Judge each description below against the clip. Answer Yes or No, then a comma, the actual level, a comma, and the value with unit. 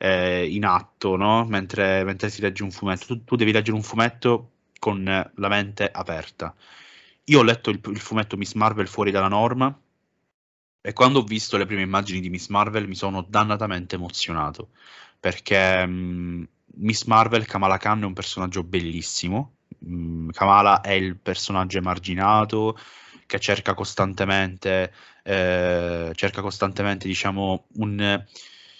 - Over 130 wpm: Yes, average, 140 wpm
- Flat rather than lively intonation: Yes, narrow, 2.2 semitones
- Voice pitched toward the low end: Yes, low, 100 Hz